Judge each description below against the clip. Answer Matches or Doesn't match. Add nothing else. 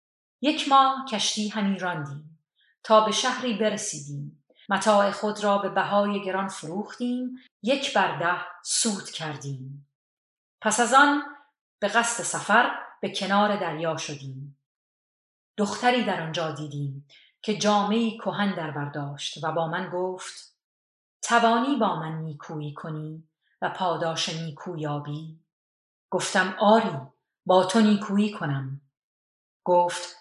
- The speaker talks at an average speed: Matches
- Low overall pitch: Doesn't match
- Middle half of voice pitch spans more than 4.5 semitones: Matches